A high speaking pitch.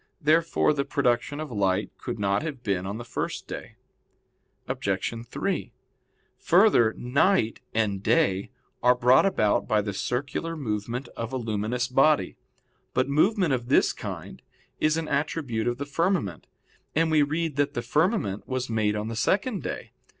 No: low, 125 Hz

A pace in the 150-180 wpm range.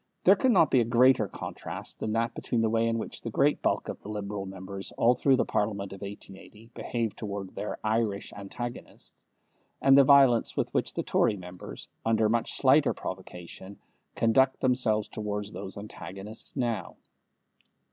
Yes: average, 165 wpm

